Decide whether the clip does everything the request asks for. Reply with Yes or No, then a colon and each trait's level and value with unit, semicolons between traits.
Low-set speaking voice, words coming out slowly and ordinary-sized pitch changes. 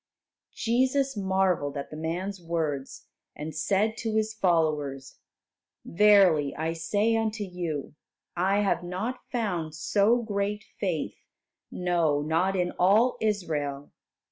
No: medium, 180 Hz; slow, 115 wpm; average, 4.8 semitones